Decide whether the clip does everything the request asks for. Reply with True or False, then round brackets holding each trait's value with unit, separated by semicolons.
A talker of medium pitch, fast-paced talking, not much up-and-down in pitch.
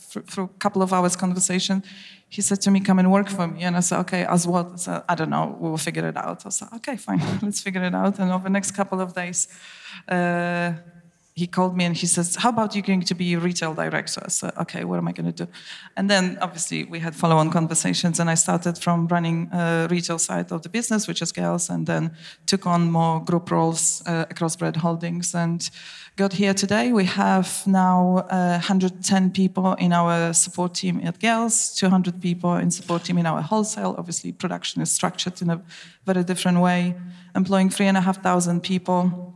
True (180 Hz; 220 wpm; 1.8 semitones)